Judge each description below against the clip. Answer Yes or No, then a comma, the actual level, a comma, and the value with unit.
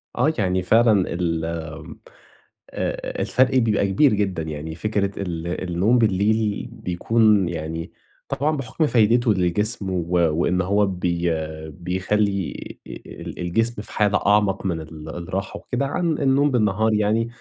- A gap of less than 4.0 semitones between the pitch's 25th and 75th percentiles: No, average, 4.4 semitones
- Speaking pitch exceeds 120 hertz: No, low, 100 Hz